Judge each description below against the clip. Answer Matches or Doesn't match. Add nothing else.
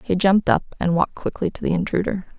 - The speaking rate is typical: Doesn't match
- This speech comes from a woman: Matches